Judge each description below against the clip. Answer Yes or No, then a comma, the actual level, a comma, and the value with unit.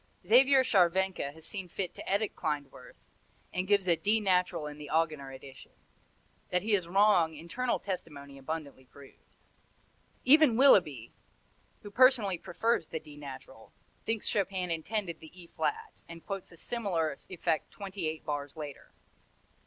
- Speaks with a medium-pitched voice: Yes, medium, 175 Hz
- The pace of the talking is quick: No, average, 145 wpm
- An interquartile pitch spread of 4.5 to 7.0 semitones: Yes, average, 4.9 semitones